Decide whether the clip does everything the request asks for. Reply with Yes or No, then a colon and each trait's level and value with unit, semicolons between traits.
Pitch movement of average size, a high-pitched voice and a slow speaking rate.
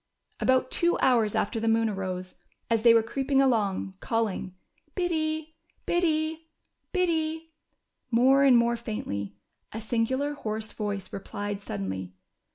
No: wide, 6.1 semitones; high, 230 Hz; slow, 125 wpm